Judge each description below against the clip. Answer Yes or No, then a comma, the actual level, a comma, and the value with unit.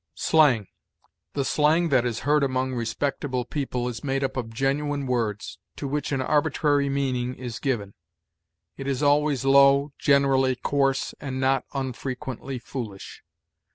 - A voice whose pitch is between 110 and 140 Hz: Yes, low, 135 Hz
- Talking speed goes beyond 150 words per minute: No, average, 140 wpm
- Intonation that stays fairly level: Yes, narrow, 2.1 semitones